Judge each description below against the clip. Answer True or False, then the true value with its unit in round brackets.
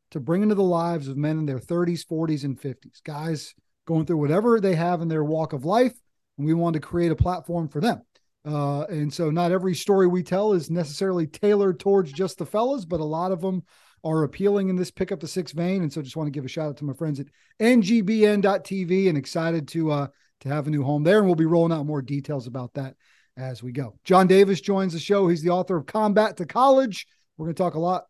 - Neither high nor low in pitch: True (170 Hz)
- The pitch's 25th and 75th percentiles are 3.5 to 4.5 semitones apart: True (4.1 semitones)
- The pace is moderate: False (245 wpm)